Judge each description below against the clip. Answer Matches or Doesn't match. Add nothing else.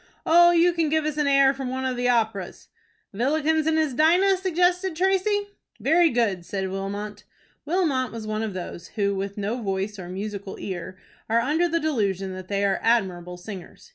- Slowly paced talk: Doesn't match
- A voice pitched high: Matches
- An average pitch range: Doesn't match